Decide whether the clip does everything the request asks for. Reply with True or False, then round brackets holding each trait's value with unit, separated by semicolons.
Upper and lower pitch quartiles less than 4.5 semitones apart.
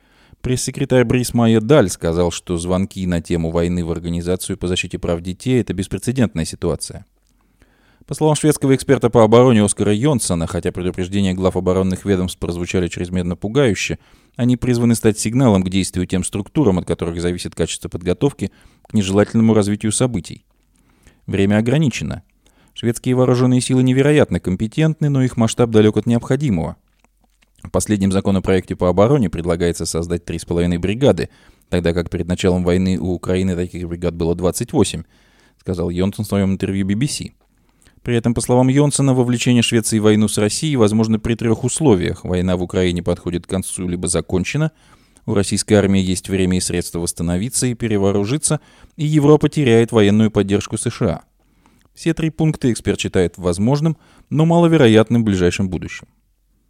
False (5.1 semitones)